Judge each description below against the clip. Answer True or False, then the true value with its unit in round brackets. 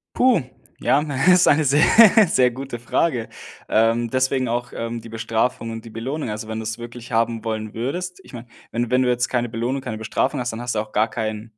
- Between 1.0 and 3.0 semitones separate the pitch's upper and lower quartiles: True (2.4 semitones)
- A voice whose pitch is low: True (120 Hz)